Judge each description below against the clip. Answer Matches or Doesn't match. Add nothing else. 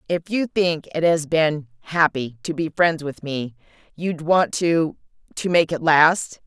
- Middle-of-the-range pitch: Matches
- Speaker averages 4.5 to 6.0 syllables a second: Doesn't match